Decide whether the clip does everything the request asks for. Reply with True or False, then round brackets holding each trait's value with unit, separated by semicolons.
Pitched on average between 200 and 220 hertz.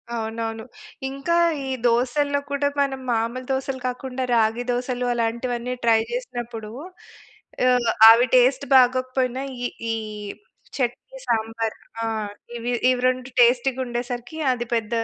False (245 Hz)